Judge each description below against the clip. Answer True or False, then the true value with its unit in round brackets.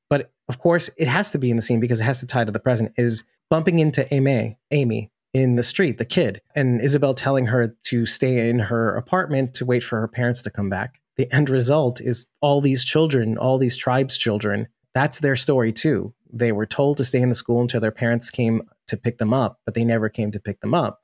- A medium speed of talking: False (240 wpm)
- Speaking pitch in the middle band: False (125 Hz)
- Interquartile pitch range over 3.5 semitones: False (2.9 semitones)